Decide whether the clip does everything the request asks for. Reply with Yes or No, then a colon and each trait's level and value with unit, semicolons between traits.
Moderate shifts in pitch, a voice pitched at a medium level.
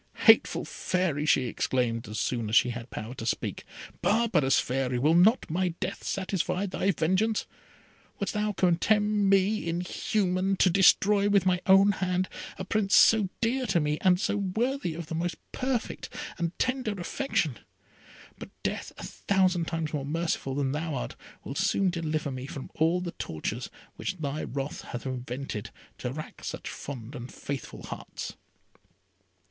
No: wide, 5.9 semitones; medium, 175 Hz